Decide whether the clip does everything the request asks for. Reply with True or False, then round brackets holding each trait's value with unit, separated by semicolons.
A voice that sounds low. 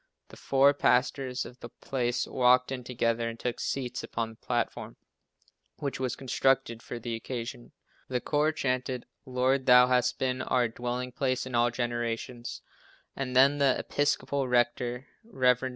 True (125 Hz)